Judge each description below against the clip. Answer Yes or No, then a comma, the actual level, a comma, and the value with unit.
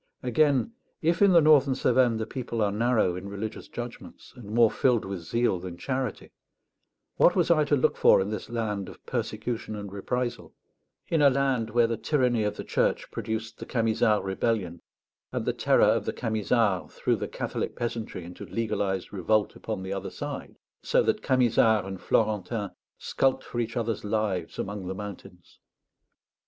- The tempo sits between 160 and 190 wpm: Yes, average, 170 wpm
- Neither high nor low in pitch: No, low, 110 Hz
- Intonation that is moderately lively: Yes, average, 3.6 semitones